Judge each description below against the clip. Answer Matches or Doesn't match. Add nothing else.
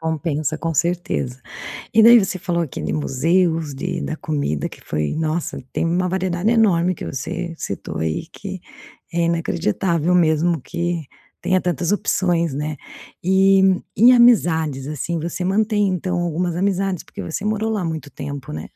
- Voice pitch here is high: Doesn't match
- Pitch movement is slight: Doesn't match